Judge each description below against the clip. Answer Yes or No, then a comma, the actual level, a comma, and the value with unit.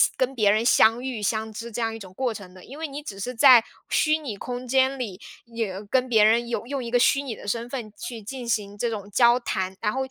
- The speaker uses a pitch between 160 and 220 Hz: No, high, 235 Hz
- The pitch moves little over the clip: No, average, 3.3 semitones